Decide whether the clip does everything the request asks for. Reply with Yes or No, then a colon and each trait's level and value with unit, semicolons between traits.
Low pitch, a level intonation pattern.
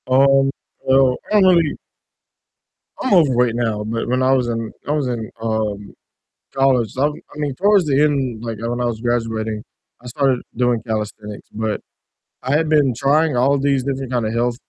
No: low, 125 Hz; average, 3.6 semitones